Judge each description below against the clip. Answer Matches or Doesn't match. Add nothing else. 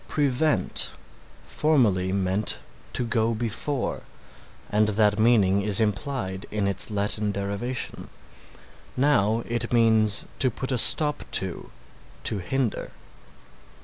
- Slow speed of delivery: Matches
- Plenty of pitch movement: Doesn't match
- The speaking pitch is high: Doesn't match